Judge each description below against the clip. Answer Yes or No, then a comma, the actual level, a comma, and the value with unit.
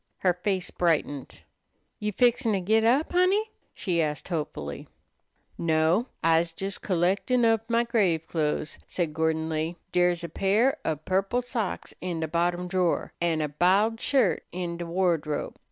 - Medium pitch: Yes, medium, 180 Hz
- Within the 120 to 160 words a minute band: Yes, average, 155 wpm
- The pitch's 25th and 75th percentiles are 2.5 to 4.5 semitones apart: No, average, 5.0 semitones